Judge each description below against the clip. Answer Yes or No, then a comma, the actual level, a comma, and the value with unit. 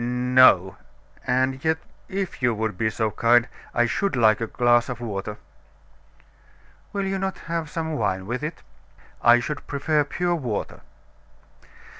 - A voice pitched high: No, low, 125 Hz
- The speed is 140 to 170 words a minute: Yes, average, 145 wpm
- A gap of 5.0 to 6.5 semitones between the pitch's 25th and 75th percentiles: Yes, wide, 5.6 semitones